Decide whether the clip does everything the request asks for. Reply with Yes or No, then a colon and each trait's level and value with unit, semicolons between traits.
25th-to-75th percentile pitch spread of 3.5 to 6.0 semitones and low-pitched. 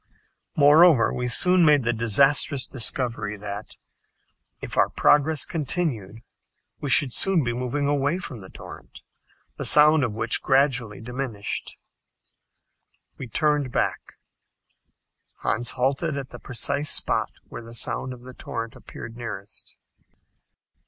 Yes: average, 4.0 semitones; low, 130 Hz